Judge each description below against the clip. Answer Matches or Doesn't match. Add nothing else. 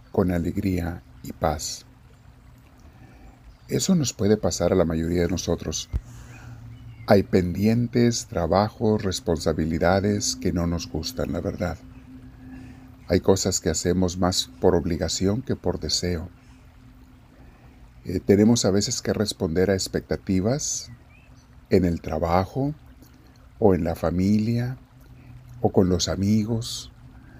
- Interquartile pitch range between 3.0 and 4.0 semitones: Doesn't match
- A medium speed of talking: Doesn't match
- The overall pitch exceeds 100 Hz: Doesn't match